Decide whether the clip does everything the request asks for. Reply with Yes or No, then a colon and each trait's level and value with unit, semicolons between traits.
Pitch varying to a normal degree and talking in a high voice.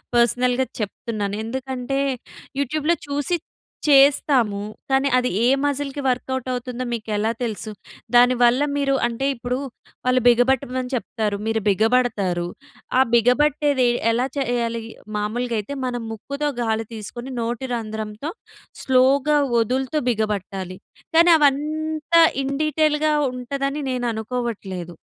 Yes: average, 3.5 semitones; very high, 250 Hz